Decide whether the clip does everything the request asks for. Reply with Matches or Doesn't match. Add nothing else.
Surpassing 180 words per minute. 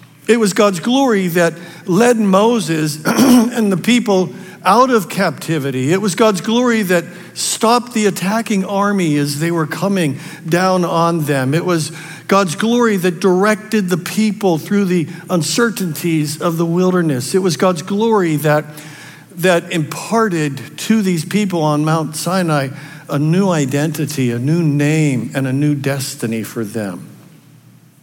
Doesn't match